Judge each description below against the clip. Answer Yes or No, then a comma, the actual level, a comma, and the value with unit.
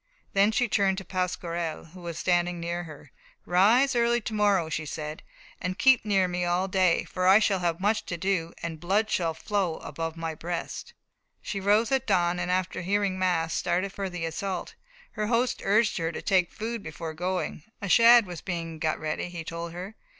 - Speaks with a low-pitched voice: No, medium, 180 Hz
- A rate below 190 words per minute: No, average, 195 wpm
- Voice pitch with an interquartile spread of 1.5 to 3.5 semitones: Yes, average, 3.2 semitones